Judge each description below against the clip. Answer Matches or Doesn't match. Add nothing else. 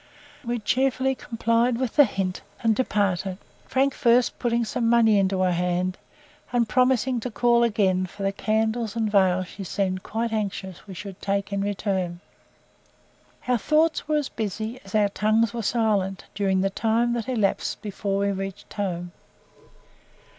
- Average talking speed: Matches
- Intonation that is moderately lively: Matches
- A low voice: Doesn't match